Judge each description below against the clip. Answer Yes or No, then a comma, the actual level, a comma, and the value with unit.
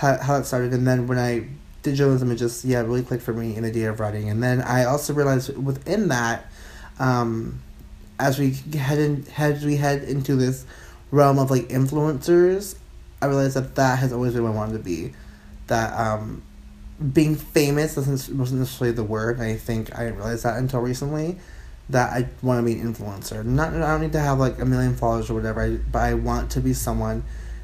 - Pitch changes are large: No, average, 3.3 semitones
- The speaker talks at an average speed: No, fast, 210 wpm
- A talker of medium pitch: No, low, 125 Hz